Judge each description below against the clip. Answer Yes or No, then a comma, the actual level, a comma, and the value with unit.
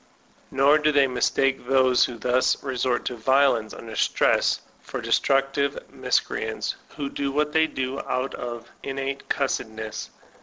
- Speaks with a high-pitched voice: No, low, 135 Hz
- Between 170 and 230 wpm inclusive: No, average, 140 wpm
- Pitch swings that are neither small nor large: No, narrow, 2.0 semitones